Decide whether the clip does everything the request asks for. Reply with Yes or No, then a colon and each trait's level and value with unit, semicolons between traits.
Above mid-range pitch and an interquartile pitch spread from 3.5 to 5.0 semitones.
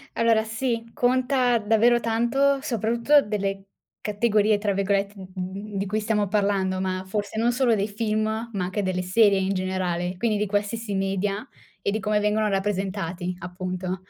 No: high, 205 Hz; average, 2.9 semitones